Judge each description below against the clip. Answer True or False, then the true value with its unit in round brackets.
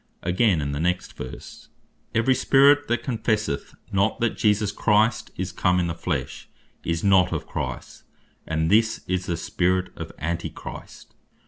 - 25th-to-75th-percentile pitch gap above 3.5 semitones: True (4.4 semitones)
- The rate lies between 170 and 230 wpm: False (150 wpm)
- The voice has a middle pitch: False (95 Hz)